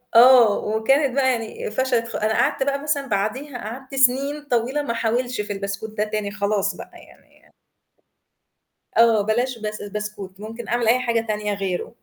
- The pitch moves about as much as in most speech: Yes, average, 3.5 semitones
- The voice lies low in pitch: No, high, 230 Hz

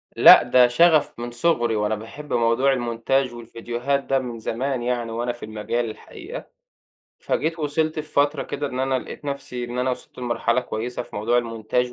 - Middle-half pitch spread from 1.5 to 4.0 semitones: Yes, average, 2.9 semitones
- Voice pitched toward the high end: No, low, 125 Hz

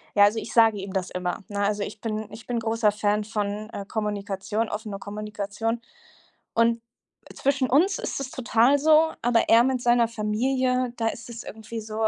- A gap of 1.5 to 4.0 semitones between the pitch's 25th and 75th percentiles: Yes, narrow, 2.4 semitones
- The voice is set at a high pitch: Yes, high, 225 Hz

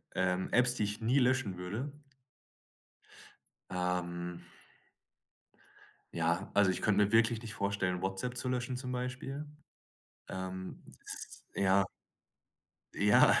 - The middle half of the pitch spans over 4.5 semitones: Yes, average, 5.1 semitones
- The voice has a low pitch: Yes, low, 100 Hz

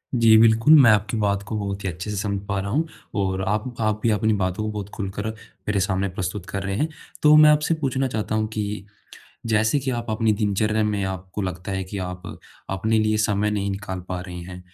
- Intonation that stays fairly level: Yes, narrow, 2.2 semitones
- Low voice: Yes, low, 105 Hz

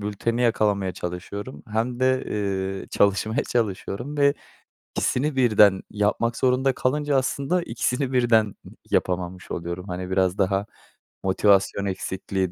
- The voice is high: No, low, 105 Hz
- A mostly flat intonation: No, average, 4.9 semitones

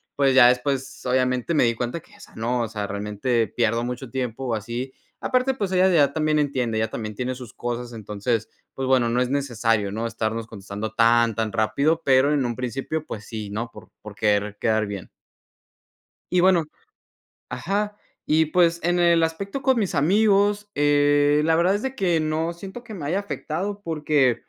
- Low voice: Yes, low, 130 Hz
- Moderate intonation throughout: No, wide, 6.3 semitones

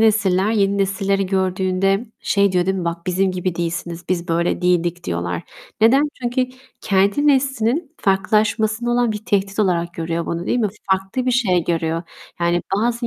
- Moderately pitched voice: No, high, 195 Hz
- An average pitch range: Yes, average, 3.9 semitones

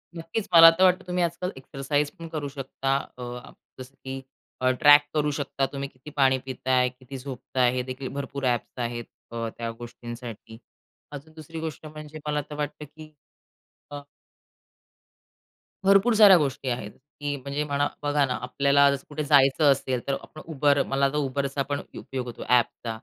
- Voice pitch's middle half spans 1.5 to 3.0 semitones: Yes, narrow, 2.6 semitones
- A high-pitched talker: No, medium, 140 Hz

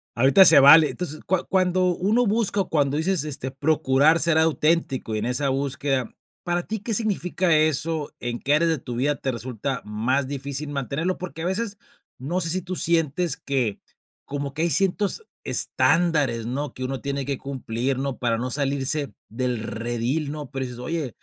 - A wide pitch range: No, average, 4.4 semitones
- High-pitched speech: No, medium, 145 Hz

